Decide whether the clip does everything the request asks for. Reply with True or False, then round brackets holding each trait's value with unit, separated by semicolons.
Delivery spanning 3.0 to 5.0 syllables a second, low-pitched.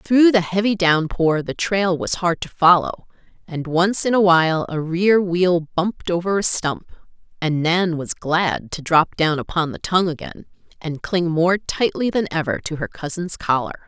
False (4.5 syllables/s; 175 Hz)